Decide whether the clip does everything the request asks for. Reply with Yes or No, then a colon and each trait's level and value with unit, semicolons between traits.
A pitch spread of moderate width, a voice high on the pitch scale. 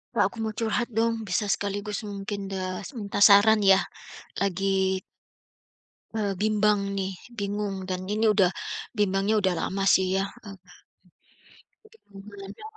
No: narrow, 1.5 semitones; high, 200 Hz